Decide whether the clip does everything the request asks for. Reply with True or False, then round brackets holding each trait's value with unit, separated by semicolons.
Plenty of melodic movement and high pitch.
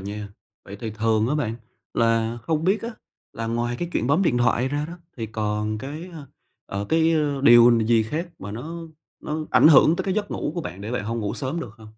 False (6.0 semitones; 120 Hz)